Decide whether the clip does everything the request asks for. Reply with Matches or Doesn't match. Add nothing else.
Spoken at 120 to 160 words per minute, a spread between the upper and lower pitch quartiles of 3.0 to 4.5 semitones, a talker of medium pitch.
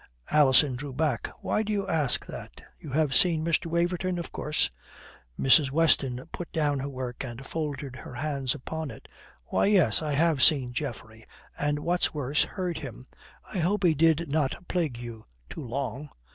Doesn't match